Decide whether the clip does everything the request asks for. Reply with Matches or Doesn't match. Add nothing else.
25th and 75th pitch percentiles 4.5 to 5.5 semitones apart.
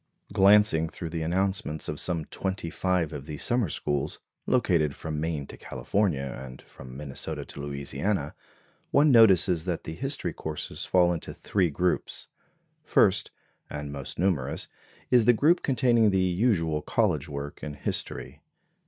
Matches